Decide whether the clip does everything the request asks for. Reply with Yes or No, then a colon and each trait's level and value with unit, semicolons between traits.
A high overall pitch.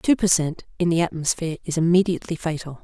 No: medium, 170 Hz